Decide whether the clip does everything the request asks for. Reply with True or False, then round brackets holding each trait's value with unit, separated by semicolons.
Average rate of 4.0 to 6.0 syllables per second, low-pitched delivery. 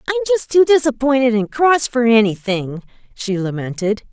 False (5.0 syllables/s; 245 Hz)